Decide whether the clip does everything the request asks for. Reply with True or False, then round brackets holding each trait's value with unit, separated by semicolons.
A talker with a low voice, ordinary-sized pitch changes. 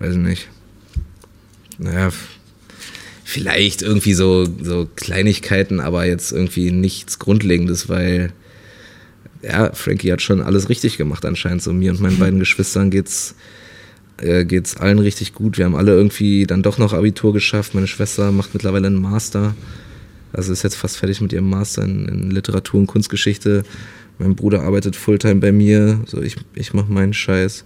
False (100 Hz; 2.0 semitones)